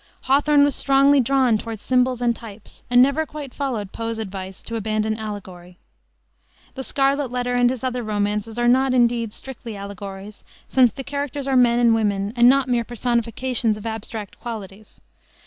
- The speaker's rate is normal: Yes, average, 165 wpm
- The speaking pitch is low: No, high, 235 Hz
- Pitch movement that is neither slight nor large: Yes, average, 3.5 semitones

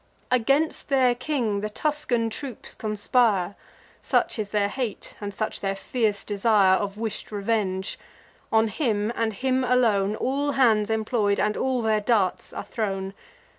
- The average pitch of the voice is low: No, high, 220 Hz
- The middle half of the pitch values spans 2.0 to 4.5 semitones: Yes, average, 3.6 semitones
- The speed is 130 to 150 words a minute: Yes, average, 145 wpm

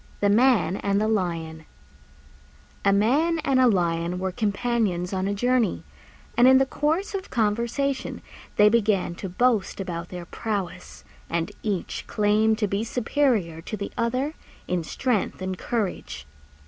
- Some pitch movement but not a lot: Yes, average, 5.0 semitones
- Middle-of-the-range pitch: No, high, 210 Hz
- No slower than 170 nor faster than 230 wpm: No, average, 150 wpm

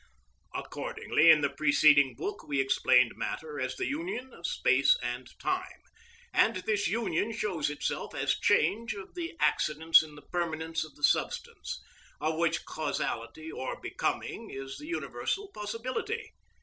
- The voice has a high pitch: No, medium, 165 Hz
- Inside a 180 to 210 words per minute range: No, average, 145 wpm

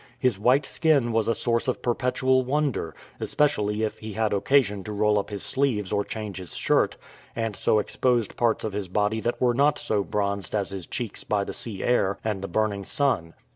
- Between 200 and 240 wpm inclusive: Yes, fast, 205 wpm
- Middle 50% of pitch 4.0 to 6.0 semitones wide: No, average, 3.5 semitones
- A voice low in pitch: Yes, low, 110 Hz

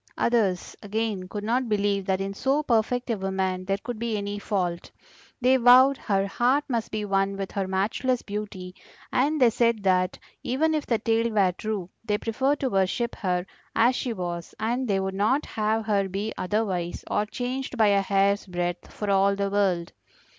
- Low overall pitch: No, high, 210 Hz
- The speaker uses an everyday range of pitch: Yes, average, 3.5 semitones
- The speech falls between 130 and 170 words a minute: No, average, 185 wpm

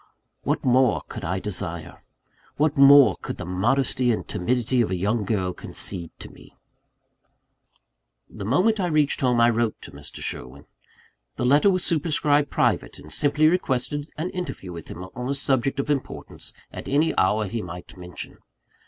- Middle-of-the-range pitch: No, low, 125 Hz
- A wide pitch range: Yes, wide, 7.0 semitones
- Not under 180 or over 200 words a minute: No, average, 165 wpm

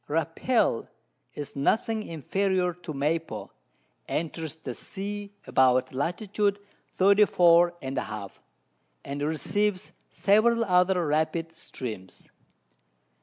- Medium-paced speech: No, slow, 95 wpm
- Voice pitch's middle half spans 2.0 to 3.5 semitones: No, average, 5.3 semitones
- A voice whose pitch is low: No, medium, 165 Hz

